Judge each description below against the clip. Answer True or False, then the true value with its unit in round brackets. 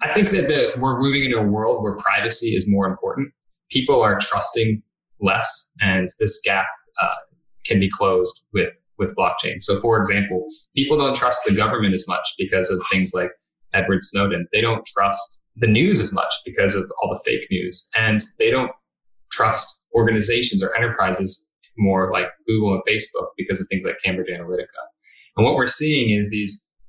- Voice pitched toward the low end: True (105 Hz)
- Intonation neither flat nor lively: True (4.2 semitones)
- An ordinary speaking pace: True (180 wpm)